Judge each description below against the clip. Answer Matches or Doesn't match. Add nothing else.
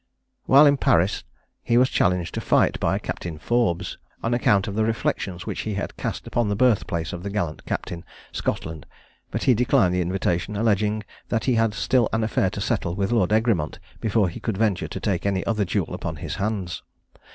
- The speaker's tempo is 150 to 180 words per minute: Doesn't match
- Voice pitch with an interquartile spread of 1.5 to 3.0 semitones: Doesn't match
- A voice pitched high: Doesn't match